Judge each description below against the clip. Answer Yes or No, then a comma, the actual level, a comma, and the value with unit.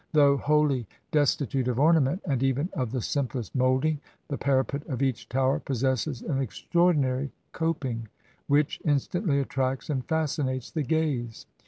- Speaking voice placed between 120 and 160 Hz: Yes, low, 135 Hz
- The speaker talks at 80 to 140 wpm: No, average, 150 wpm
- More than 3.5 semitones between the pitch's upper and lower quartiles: No, narrow, 2.6 semitones